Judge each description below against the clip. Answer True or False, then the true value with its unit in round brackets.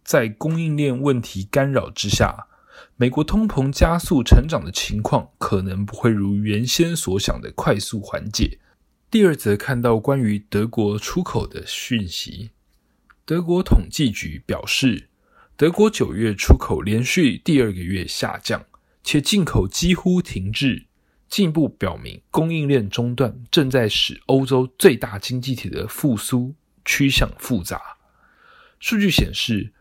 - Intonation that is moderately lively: False (6.9 semitones)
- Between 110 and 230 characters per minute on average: True (215 characters per minute)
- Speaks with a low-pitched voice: True (125 Hz)